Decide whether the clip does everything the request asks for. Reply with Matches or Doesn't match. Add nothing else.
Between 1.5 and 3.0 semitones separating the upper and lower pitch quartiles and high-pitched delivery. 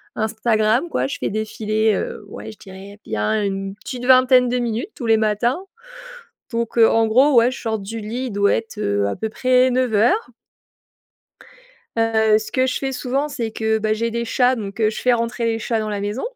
Matches